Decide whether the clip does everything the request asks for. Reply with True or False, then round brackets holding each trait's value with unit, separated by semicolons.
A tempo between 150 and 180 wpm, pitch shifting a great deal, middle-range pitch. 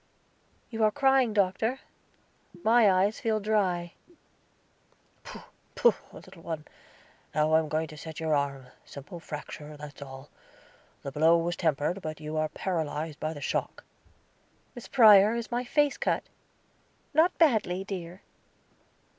False (140 wpm; 6.1 semitones; 175 Hz)